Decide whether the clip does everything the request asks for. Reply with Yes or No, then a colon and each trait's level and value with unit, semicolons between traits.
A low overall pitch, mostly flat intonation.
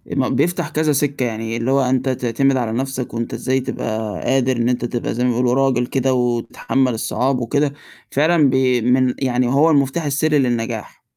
Yes: low, 130 Hz; narrow, 2.1 semitones